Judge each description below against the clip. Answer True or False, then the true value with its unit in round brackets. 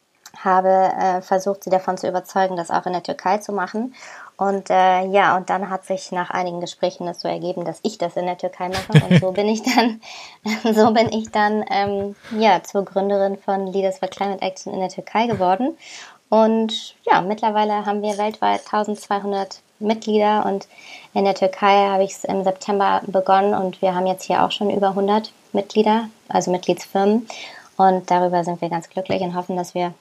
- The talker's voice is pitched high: True (195 Hz)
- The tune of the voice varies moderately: False (2.2 semitones)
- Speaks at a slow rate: False (190 wpm)